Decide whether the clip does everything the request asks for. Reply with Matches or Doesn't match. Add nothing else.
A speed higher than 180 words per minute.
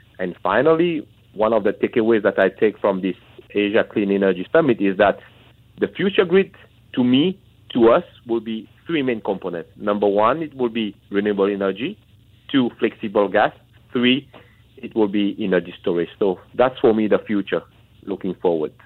Doesn't match